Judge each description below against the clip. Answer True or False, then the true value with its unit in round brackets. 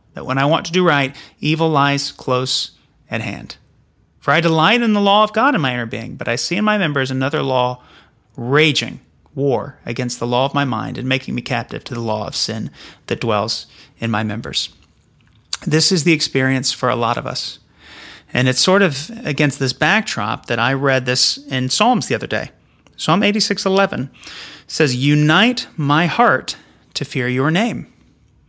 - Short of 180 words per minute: False (190 wpm)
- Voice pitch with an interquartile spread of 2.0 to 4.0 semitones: False (4.5 semitones)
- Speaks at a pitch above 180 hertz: False (140 Hz)